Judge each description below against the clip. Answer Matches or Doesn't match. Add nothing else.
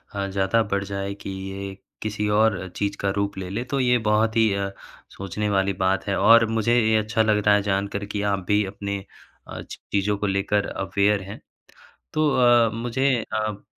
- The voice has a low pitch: Matches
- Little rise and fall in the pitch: Matches